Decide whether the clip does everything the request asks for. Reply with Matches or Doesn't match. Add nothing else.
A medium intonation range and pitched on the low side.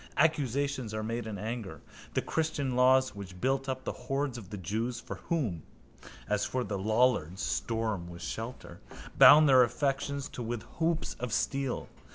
Matches